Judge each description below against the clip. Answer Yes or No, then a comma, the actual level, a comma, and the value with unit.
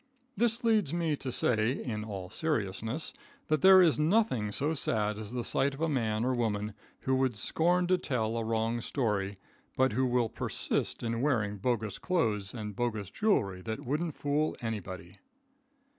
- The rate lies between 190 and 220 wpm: No, average, 170 wpm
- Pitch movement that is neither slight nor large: No, wide, 6.1 semitones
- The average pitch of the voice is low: Yes, low, 120 Hz